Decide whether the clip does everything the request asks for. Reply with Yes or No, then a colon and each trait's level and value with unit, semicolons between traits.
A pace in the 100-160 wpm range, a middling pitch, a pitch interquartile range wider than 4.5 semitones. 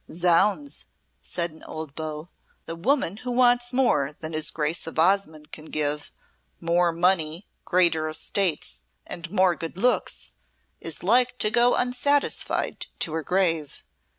Yes: average, 140 wpm; medium, 170 Hz; average, 5.2 semitones